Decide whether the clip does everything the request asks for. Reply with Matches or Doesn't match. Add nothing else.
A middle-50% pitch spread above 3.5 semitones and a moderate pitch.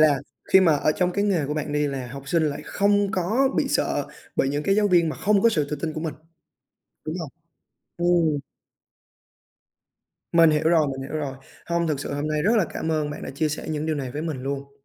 Doesn't match